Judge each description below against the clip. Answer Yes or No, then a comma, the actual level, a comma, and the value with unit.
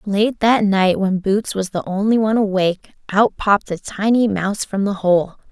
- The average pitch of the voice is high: Yes, high, 200 Hz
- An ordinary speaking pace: Yes, average, 195 wpm